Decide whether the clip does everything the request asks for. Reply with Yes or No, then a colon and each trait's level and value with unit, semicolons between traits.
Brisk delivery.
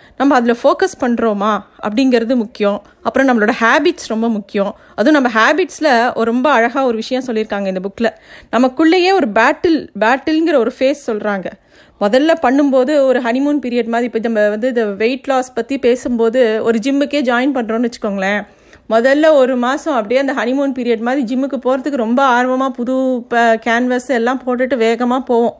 Yes: fast, 150 wpm